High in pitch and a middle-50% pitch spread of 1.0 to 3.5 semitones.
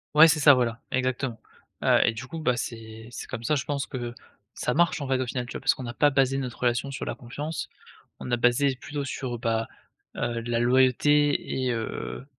No: low, 130 Hz; average, 2.8 semitones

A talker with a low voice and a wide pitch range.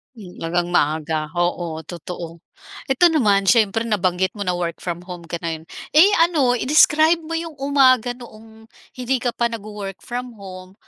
No: high, 210 Hz; wide, 6.2 semitones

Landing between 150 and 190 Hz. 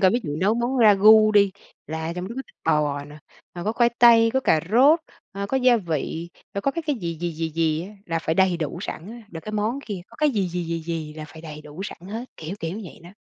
Yes: medium, 185 Hz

